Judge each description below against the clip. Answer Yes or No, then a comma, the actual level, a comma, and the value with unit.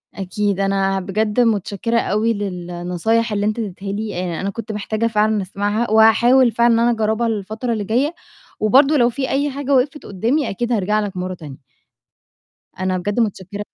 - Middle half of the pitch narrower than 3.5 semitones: Yes, average, 3.1 semitones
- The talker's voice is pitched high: Yes, high, 215 Hz